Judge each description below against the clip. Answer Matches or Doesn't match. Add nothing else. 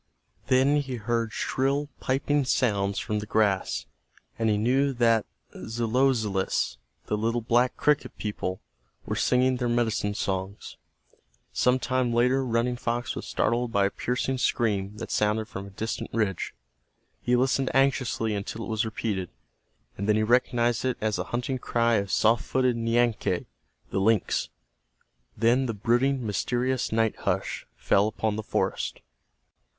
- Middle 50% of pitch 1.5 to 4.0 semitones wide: Matches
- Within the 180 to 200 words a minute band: Doesn't match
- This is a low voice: Matches